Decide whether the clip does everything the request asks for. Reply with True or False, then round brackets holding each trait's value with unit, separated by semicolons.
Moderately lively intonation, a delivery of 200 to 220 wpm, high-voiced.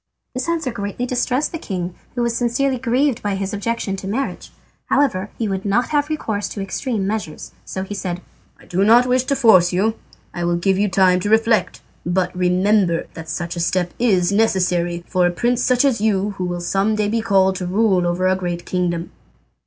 True (4.4 semitones; 205 wpm; 200 Hz)